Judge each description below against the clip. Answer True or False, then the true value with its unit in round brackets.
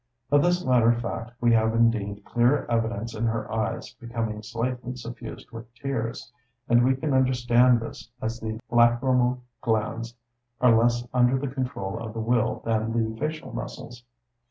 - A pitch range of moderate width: False (1.7 semitones)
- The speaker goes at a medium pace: True (155 wpm)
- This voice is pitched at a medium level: False (120 Hz)